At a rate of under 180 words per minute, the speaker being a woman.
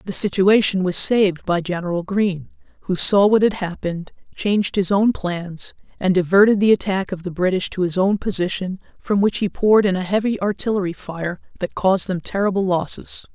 No: average, 185 wpm; female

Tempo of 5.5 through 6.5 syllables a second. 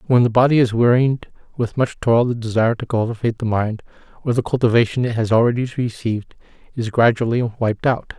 Yes: 6.1 syllables/s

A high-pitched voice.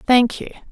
Yes: high, 245 Hz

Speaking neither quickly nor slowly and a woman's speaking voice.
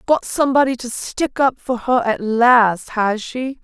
Yes: average, 180 wpm; female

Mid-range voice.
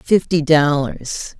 Yes: medium, 155 Hz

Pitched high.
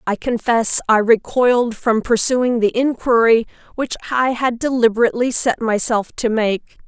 Yes: high, 235 Hz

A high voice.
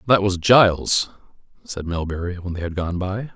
No: very low, 95 Hz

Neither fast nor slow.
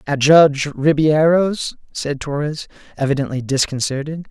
No: slow, 100 wpm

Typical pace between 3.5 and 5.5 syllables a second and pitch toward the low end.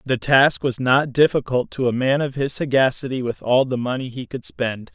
Yes: 5.0 syllables/s; low, 130 Hz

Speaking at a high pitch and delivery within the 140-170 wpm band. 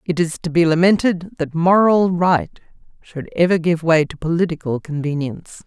No: medium, 165 Hz; average, 160 wpm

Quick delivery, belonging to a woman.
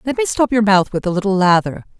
Yes: fast, 270 wpm; female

